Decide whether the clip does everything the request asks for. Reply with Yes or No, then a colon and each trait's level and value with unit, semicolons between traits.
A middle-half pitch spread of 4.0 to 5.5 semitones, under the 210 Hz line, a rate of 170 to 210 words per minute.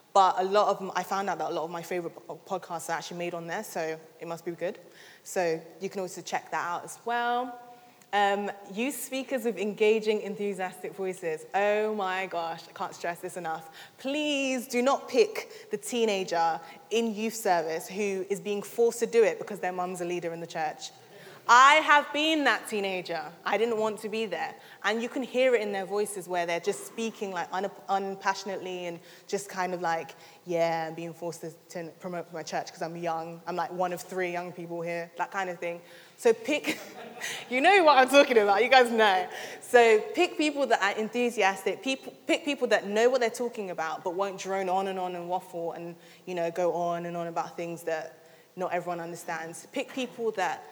Yes: average, 4.8 semitones; high, 190 Hz; fast, 205 wpm